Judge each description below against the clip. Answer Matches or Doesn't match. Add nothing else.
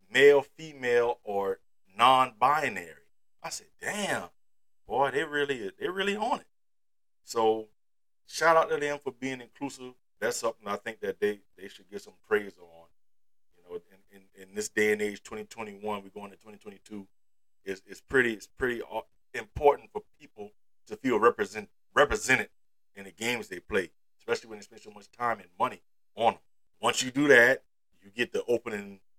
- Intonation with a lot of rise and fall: Matches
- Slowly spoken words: Doesn't match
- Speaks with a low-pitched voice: Matches